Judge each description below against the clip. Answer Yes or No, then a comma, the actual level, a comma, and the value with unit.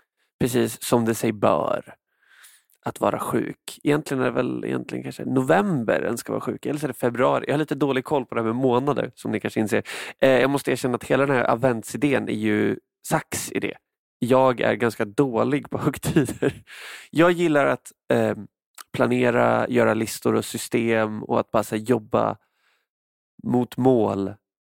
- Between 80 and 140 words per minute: No, average, 175 wpm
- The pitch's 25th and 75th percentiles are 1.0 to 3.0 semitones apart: No, average, 3.6 semitones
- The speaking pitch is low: Yes, low, 120 Hz